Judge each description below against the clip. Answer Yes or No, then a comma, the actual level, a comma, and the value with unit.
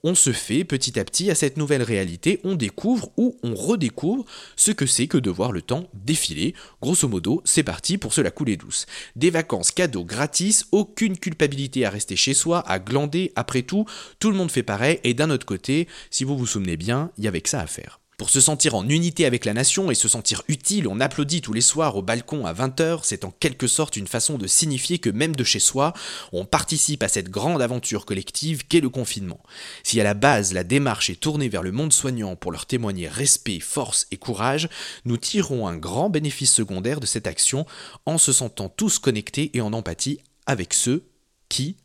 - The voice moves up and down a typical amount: No, wide, 6.0 semitones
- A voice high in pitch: No, low, 135 Hz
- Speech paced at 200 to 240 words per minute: Yes, average, 215 wpm